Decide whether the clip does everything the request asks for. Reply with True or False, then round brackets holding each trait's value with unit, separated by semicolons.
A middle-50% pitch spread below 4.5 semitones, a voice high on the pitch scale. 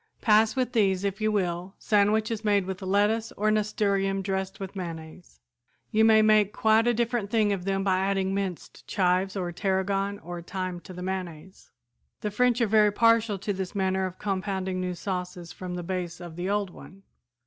True (2.4 semitones; 195 Hz)